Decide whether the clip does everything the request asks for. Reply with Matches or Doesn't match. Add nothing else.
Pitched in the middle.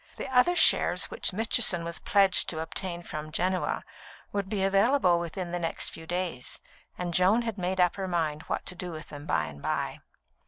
Matches